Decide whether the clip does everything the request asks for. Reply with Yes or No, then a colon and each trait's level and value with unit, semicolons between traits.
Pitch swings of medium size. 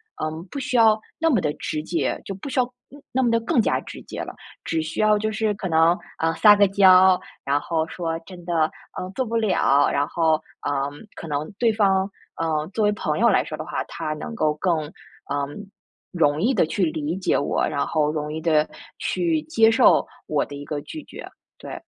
No: wide, 5.8 semitones